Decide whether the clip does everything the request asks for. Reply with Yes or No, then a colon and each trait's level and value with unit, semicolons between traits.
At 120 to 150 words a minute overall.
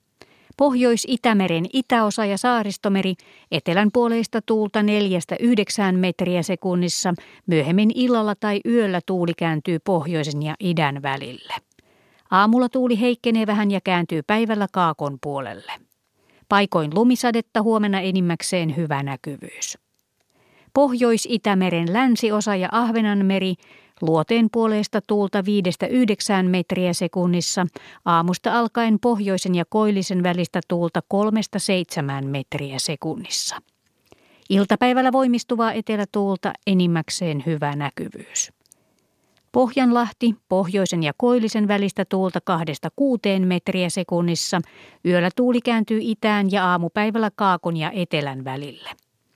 No: slow, 95 wpm